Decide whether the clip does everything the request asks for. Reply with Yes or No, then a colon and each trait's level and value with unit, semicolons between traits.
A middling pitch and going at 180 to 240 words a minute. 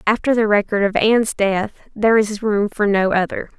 No: high, 210 Hz; average, 200 wpm